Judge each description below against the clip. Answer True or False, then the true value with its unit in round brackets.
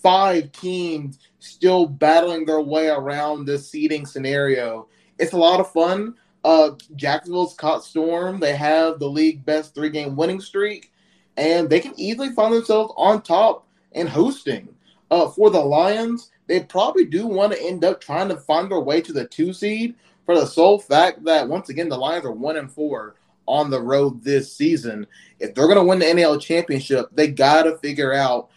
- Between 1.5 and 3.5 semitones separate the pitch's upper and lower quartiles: False (4.2 semitones)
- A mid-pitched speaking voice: True (160 Hz)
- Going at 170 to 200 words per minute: True (185 wpm)